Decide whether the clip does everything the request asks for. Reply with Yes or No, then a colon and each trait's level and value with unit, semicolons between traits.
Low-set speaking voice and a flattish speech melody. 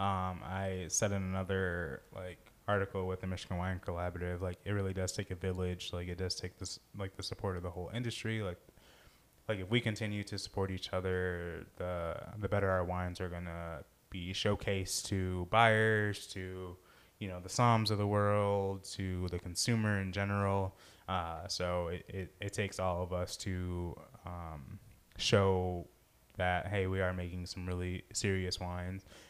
Yes: very low, 95 Hz; narrow, 1.9 semitones